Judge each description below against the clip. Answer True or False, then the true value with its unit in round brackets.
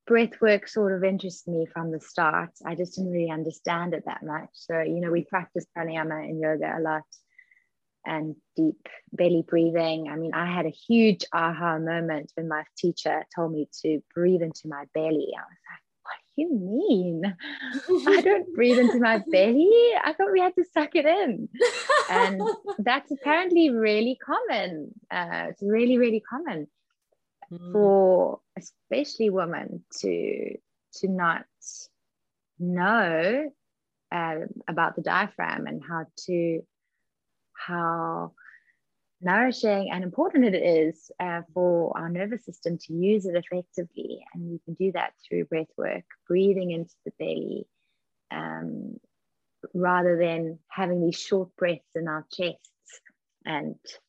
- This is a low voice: False (180 Hz)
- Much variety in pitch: True (6.1 semitones)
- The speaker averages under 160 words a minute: True (145 wpm)